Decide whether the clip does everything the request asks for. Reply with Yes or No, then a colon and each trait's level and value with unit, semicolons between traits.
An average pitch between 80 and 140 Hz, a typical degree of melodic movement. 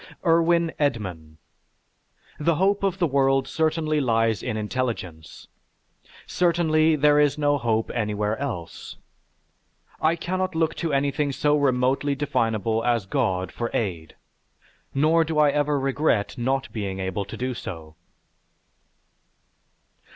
No: low, 135 Hz; wide, 5.9 semitones